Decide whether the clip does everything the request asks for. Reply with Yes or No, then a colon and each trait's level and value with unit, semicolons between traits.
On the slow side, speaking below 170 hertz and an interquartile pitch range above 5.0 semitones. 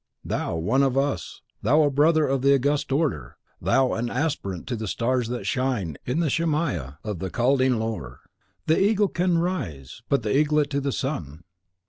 No: average, 180 wpm; low, 135 Hz; wide, 5.4 semitones